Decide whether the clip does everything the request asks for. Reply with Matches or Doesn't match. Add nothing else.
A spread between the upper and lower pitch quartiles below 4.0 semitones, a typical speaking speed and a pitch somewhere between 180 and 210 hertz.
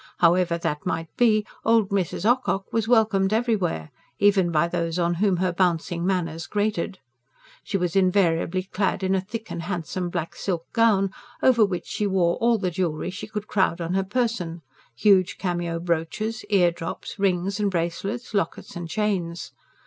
Matches